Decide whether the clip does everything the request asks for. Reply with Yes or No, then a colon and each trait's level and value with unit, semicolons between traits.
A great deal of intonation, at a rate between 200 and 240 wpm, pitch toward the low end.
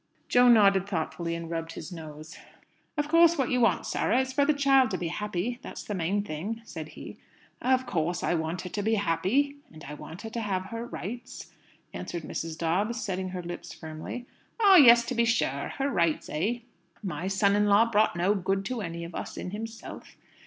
No: wide, 5.9 semitones; fast, 205 wpm; high, 200 Hz